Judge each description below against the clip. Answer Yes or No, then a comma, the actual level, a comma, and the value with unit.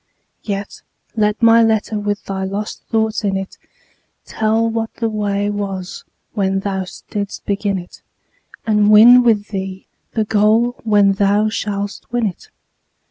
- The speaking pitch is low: No, high, 210 Hz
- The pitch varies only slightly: Yes, narrow, 1.8 semitones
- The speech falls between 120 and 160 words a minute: Yes, average, 140 wpm